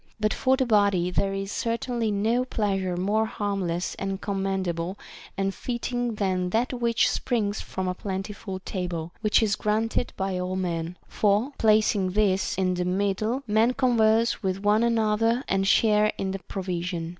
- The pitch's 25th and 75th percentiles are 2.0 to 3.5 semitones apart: Yes, average, 3.0 semitones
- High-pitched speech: Yes, high, 200 Hz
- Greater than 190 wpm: No, average, 170 wpm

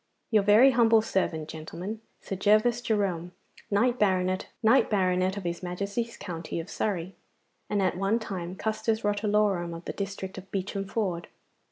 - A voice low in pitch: No, high, 195 Hz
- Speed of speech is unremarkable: Yes, average, 145 wpm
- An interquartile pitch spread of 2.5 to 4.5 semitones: Yes, average, 2.9 semitones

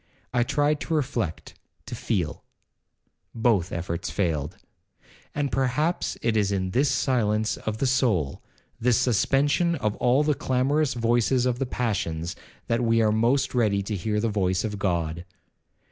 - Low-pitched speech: Yes, low, 115 Hz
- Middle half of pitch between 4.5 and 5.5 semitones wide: Yes, average, 4.9 semitones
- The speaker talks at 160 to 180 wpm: No, average, 145 wpm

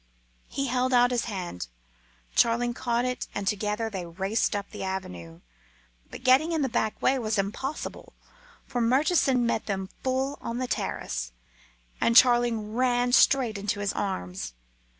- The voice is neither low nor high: No, high, 230 Hz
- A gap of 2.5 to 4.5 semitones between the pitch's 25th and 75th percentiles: Yes, average, 4.2 semitones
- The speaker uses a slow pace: No, average, 155 wpm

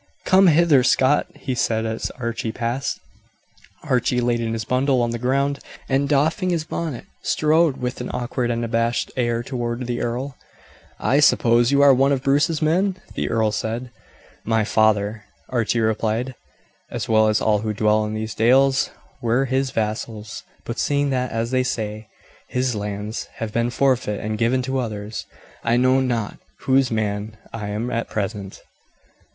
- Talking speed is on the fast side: No, average, 165 wpm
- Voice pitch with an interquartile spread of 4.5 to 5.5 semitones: No, average, 3.2 semitones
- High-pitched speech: No, low, 120 Hz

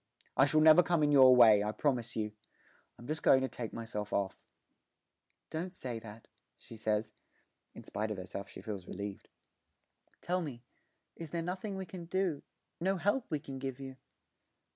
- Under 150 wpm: No, average, 175 wpm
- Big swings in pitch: Yes, wide, 7.3 semitones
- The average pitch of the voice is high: No, low, 135 Hz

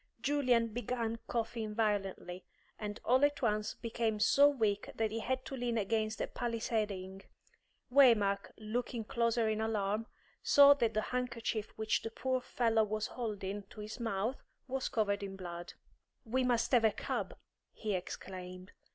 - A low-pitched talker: No, high, 225 Hz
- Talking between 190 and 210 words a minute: No, average, 150 wpm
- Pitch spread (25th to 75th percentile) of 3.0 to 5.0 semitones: No, narrow, 2.6 semitones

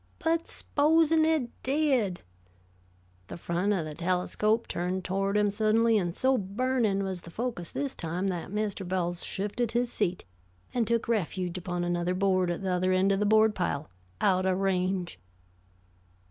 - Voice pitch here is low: No, high, 195 Hz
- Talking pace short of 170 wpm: Yes, average, 160 wpm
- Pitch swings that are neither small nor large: Yes, average, 4.2 semitones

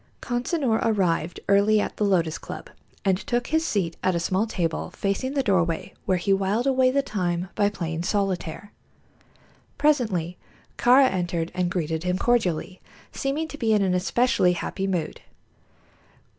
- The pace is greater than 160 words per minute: No, average, 155 wpm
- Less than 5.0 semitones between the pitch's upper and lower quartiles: No, wide, 5.5 semitones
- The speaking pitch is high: Yes, high, 195 Hz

